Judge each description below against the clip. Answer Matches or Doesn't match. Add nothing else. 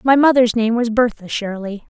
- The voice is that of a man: Doesn't match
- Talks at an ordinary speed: Matches